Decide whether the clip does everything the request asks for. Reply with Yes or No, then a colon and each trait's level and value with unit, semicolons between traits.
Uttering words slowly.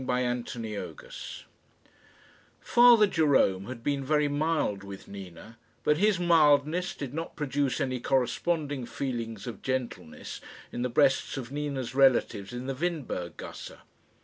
Yes: slow, 130 wpm